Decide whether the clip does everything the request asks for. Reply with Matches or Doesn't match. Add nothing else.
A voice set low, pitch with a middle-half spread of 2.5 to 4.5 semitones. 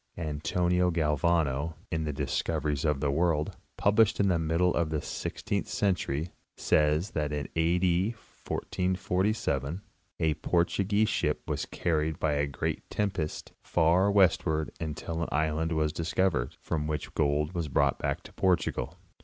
Matches